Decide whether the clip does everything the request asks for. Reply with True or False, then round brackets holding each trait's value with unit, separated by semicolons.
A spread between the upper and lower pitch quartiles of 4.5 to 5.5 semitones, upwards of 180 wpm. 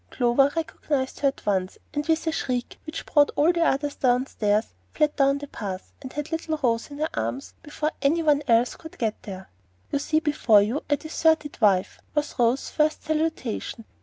True (5.0 semitones; 190 wpm)